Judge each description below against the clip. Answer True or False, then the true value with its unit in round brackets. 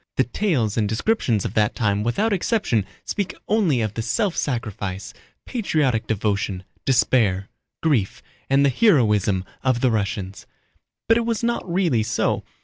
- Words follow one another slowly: False (145 wpm)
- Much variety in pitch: True (9.0 semitones)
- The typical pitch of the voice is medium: False (120 Hz)